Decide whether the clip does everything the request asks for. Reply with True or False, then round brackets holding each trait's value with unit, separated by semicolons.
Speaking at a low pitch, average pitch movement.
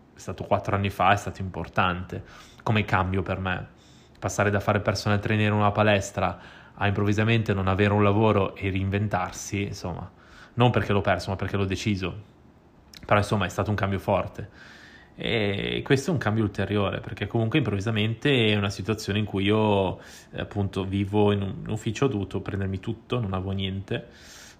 False (100 Hz; 1.8 semitones)